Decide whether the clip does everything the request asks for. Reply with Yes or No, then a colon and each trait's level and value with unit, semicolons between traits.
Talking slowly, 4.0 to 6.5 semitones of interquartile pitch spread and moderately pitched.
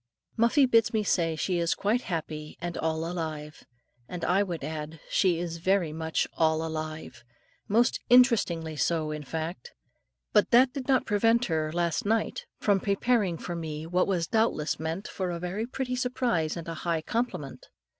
No: average, 170 wpm; average, 5.1 semitones; medium, 170 Hz